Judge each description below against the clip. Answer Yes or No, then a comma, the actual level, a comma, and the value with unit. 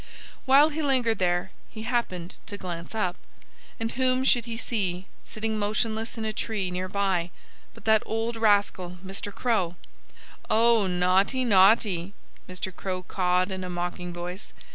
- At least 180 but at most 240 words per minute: No, average, 150 wpm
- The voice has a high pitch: Yes, high, 200 Hz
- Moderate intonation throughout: Yes, average, 3.8 semitones